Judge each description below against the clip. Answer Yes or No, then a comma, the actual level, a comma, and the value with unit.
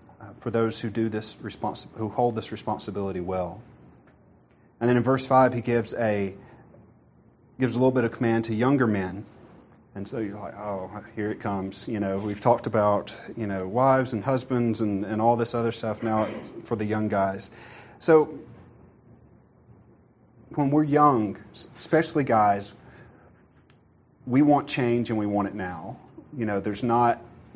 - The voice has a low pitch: Yes, low, 115 Hz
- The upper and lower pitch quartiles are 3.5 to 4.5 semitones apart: No, average, 2.7 semitones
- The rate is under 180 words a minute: Yes, average, 170 wpm